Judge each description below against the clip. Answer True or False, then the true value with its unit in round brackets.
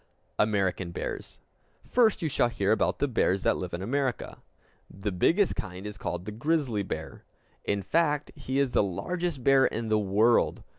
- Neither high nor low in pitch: False (110 Hz)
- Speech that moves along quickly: False (170 wpm)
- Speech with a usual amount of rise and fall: False (6.4 semitones)